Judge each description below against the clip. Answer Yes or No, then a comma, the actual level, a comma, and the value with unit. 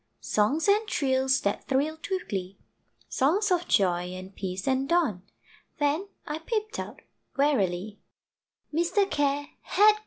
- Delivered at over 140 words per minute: No, slow, 135 wpm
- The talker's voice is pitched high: Yes, very high, 285 Hz